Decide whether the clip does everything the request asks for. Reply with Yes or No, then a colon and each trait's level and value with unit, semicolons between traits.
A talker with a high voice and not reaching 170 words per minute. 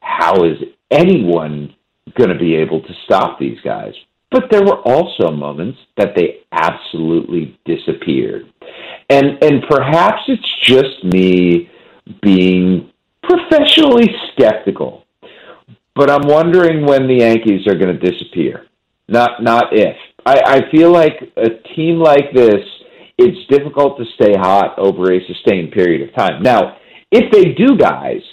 No: medium, 140 Hz; average, 140 wpm